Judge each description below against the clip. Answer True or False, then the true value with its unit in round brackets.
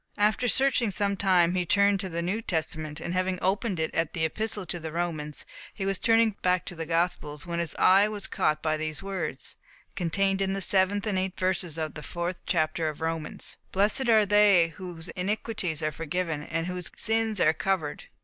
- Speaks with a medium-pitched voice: True (180 Hz)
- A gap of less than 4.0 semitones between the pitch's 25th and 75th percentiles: True (3.5 semitones)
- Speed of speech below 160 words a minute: False (195 wpm)